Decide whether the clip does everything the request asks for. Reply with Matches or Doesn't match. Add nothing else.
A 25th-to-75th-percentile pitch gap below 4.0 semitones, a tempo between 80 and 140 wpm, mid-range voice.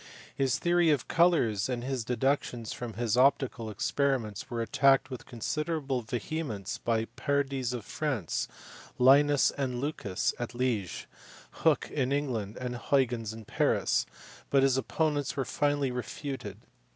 Doesn't match